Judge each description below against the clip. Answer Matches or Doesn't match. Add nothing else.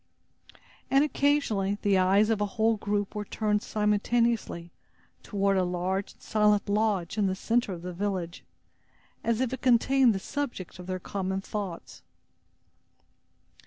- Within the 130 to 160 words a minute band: Matches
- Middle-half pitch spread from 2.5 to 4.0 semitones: Matches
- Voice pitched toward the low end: Doesn't match